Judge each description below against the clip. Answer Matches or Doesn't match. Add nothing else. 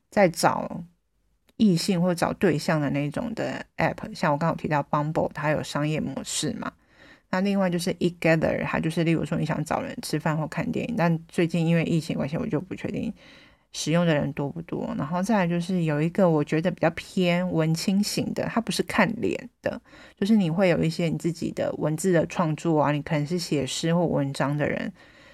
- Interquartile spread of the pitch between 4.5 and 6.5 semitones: Doesn't match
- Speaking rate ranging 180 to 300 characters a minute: Doesn't match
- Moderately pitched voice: Matches